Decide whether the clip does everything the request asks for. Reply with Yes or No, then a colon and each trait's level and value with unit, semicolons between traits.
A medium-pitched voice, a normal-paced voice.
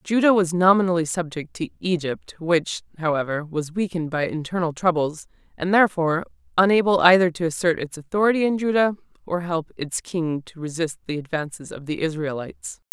Yes: medium, 170 Hz; average, 160 wpm